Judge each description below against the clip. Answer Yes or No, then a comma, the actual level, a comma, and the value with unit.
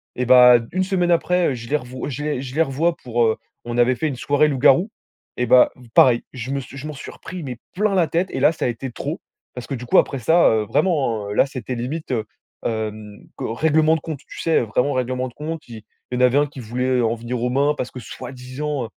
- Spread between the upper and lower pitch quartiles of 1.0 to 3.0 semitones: No, average, 3.8 semitones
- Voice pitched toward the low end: Yes, low, 130 Hz